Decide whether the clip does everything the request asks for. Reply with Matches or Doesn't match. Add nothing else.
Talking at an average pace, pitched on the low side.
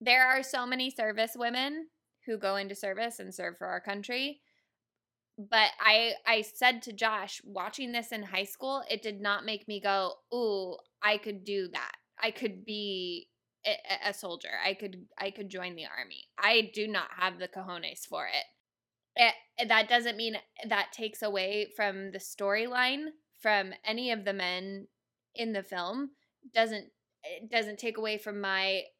Doesn't match